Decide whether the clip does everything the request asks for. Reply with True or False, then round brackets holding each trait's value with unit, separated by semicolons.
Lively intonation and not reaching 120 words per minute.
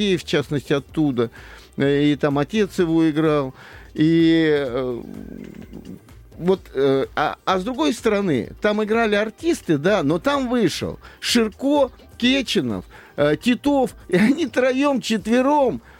True (8.9 semitones; 110 wpm)